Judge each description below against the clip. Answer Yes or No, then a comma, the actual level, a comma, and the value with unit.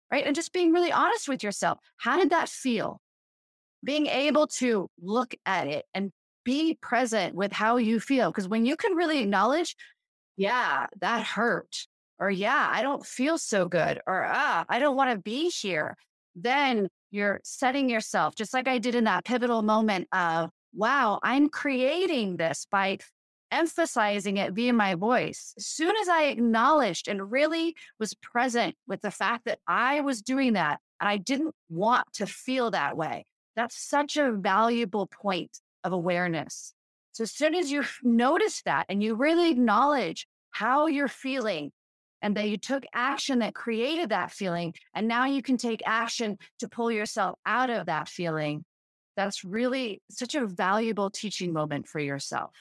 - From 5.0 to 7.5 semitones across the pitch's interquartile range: Yes, wide, 5.6 semitones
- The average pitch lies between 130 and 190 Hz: No, high, 235 Hz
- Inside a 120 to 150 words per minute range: No, average, 170 wpm